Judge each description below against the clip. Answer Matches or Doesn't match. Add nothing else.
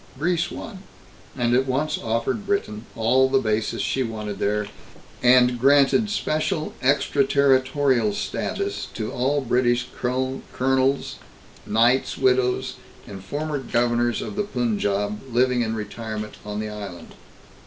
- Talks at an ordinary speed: Doesn't match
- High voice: Doesn't match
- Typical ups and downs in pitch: Matches